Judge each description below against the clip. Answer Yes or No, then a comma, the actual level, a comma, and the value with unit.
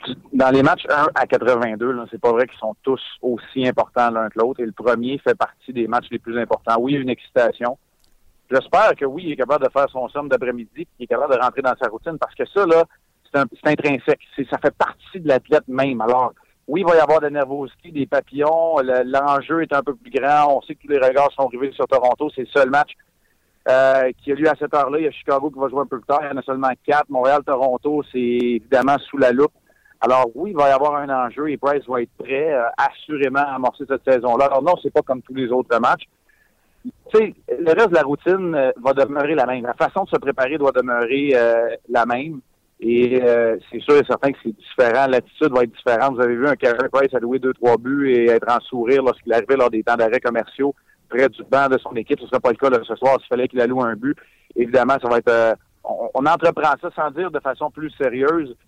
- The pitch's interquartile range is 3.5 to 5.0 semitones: No, average, 2.9 semitones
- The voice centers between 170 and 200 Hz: No, low, 135 Hz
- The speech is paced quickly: Yes, fast, 255 wpm